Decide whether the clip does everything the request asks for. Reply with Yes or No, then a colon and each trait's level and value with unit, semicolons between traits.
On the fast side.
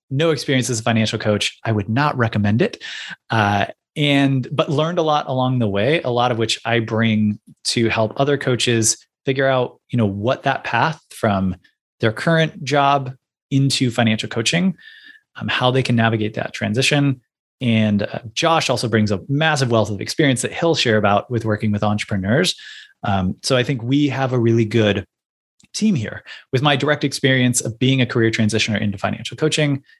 No: average, 185 wpm